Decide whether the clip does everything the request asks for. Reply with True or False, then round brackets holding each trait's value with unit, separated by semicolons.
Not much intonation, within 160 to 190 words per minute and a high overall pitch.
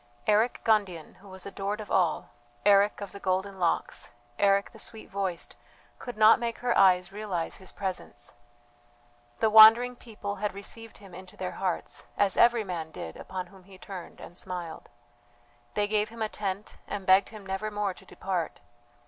True (2.3 semitones; 175 wpm; 200 Hz)